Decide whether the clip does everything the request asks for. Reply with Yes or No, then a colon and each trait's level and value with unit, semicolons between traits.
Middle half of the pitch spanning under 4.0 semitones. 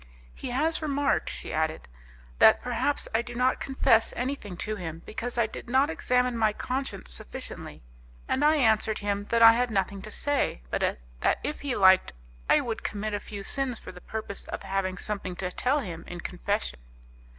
No: average, 4.8 semitones